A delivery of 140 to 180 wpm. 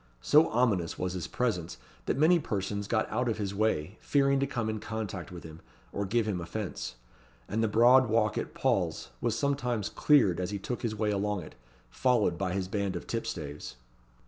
No: average, 195 wpm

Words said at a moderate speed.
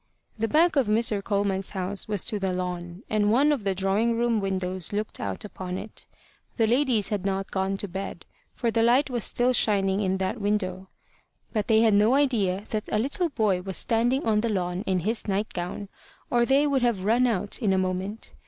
No: fast, 210 wpm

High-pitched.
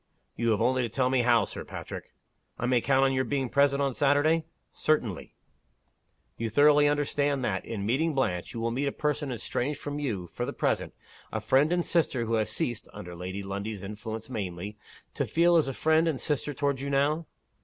No: low, 130 Hz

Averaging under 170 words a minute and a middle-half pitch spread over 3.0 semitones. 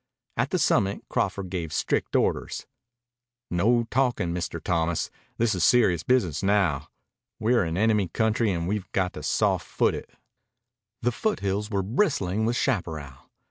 Yes: average, 145 wpm; average, 4.6 semitones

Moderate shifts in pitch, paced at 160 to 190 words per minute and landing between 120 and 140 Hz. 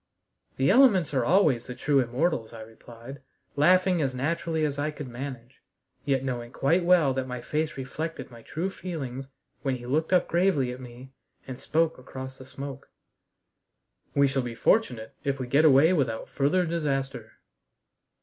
Yes: average, 4.0 semitones; average, 165 wpm; low, 135 Hz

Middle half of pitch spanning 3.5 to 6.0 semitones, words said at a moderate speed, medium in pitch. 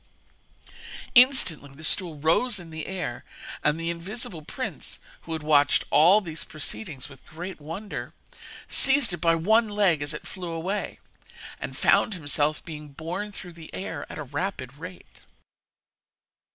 Yes: average, 4.1 semitones; average, 150 wpm; medium, 165 Hz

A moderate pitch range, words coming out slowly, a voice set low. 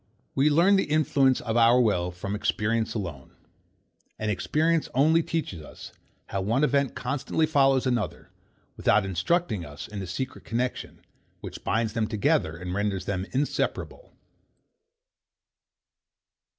No: wide, 6.2 semitones; slow, 130 wpm; low, 115 Hz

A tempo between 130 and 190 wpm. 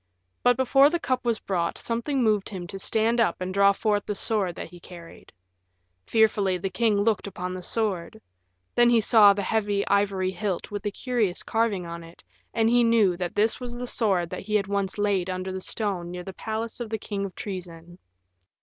No: fast, 205 wpm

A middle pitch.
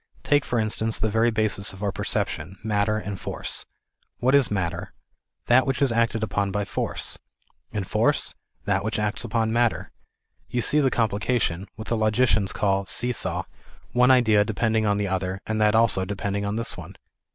No: low, 110 Hz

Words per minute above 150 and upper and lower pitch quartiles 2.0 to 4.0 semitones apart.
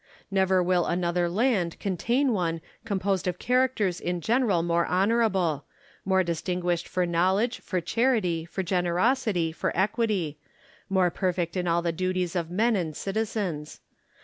No: average, 145 wpm; average, 3.3 semitones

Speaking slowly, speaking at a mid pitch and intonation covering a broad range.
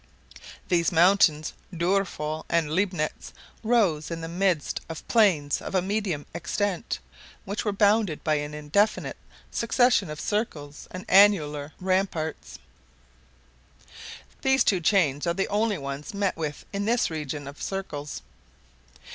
No: slow, 130 wpm; medium, 175 Hz; average, 4.8 semitones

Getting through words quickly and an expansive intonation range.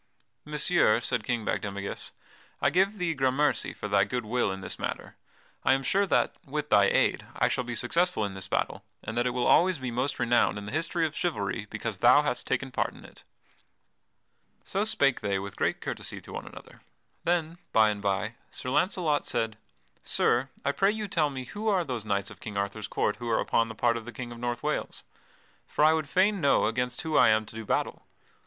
Yes: fast, 215 wpm; wide, 6.2 semitones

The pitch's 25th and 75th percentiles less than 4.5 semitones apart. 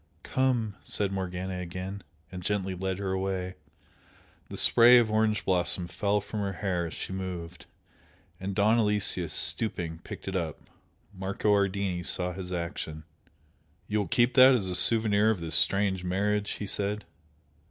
Yes: narrow, 2.4 semitones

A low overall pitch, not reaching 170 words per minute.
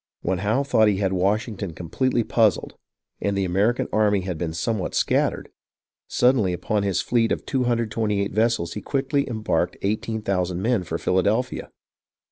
Yes: low, 105 Hz; average, 155 wpm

